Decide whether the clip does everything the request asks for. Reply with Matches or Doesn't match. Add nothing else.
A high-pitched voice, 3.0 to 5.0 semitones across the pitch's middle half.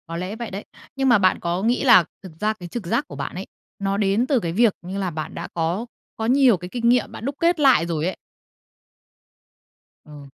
Doesn't match